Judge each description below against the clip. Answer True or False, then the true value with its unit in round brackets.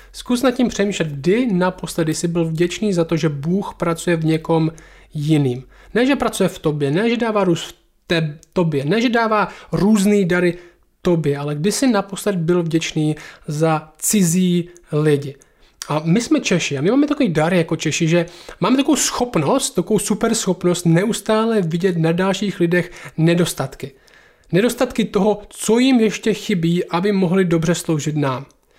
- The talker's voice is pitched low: False (175 Hz)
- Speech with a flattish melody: False (4.4 semitones)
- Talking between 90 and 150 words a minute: False (165 wpm)